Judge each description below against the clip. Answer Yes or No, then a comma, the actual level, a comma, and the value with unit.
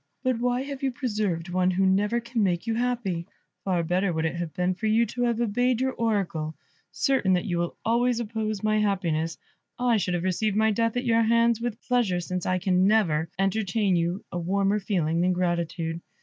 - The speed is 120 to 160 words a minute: No, fast, 205 wpm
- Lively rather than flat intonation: No, average, 4.7 semitones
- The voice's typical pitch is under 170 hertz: No, high, 200 Hz